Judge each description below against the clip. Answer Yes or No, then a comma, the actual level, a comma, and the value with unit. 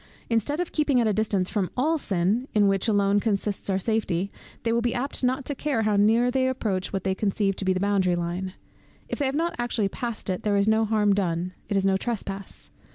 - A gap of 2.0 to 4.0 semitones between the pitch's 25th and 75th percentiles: Yes, average, 3.7 semitones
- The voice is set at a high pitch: Yes, high, 210 Hz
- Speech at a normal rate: No, fast, 230 wpm